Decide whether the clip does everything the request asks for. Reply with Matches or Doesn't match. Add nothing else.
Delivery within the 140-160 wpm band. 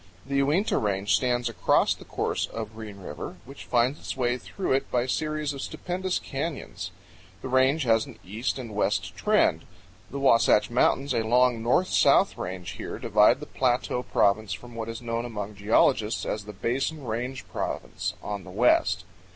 Doesn't match